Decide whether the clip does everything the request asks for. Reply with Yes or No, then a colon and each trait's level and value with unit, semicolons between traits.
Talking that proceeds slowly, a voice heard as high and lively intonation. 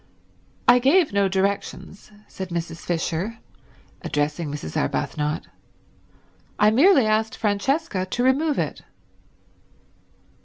Yes: slow, 100 wpm; high, 200 Hz; wide, 6.5 semitones